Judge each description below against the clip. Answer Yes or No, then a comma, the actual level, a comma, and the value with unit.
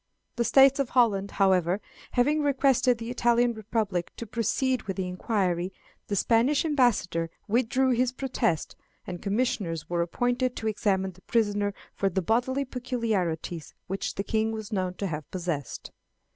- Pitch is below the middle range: No, high, 220 Hz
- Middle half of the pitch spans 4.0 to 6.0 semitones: Yes, average, 4.8 semitones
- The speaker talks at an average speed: Yes, average, 150 wpm